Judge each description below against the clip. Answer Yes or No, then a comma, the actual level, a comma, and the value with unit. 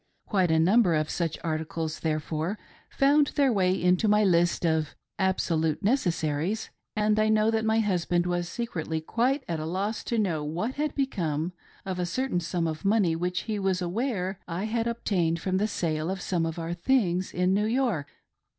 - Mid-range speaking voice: Yes, medium, 180 Hz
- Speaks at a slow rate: No, average, 185 wpm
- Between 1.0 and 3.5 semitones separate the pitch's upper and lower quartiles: No, average, 4.6 semitones